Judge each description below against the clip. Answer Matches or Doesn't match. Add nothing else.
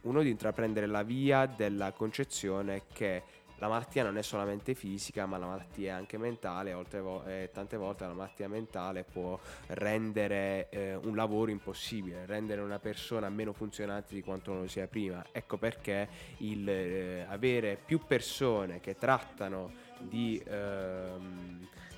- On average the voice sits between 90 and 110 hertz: Matches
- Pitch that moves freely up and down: Doesn't match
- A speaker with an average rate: Matches